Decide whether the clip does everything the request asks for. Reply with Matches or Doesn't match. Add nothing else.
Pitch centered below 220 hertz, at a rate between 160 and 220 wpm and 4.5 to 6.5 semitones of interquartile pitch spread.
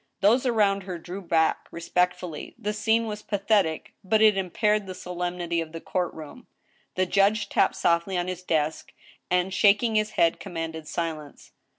Doesn't match